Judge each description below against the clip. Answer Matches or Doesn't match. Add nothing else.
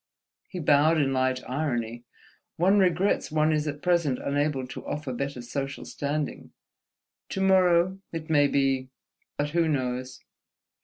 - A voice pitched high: Doesn't match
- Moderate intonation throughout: Matches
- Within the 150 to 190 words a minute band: Doesn't match